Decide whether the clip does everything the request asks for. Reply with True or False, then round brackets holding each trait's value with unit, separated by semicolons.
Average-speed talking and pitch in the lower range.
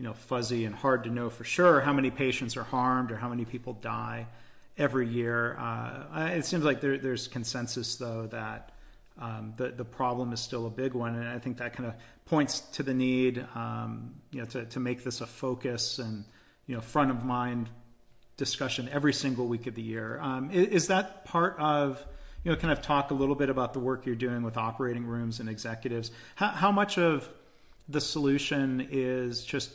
False (210 wpm; 125 Hz)